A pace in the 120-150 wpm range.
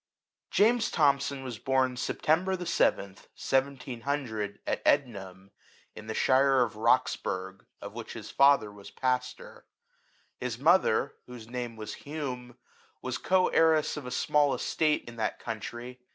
Yes: average, 140 wpm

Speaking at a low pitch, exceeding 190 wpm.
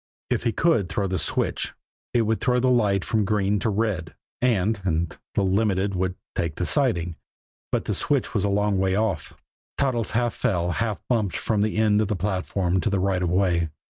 Yes: low, 100 Hz; average, 200 wpm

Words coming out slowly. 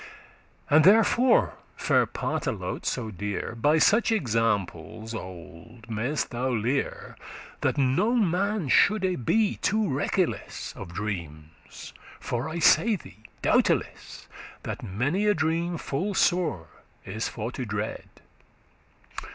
Yes: slow, 120 wpm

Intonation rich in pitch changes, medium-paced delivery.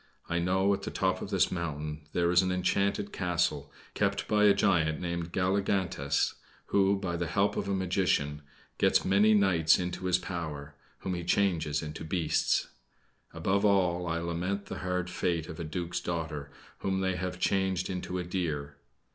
No: narrow, 2.6 semitones; average, 170 wpm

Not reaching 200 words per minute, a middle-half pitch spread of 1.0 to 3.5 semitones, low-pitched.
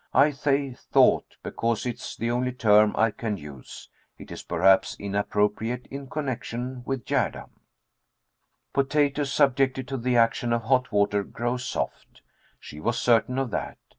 No: average, 150 wpm; average, 3.9 semitones; low, 120 Hz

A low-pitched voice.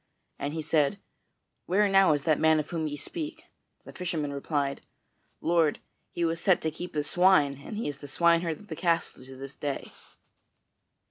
No: medium, 160 Hz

